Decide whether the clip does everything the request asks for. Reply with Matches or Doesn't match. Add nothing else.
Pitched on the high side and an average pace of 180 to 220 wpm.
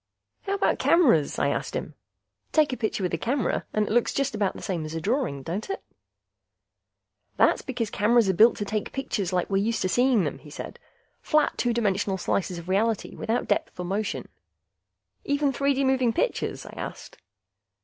Matches